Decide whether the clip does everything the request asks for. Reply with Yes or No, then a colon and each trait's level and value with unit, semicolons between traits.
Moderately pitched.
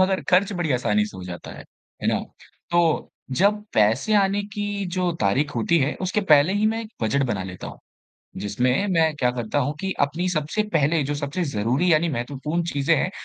Yes: medium, 155 Hz